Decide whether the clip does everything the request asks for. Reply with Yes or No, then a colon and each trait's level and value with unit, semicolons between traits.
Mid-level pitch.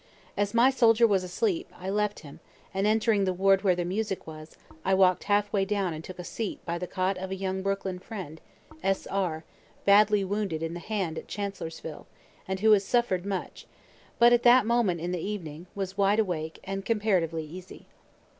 No: high, 195 Hz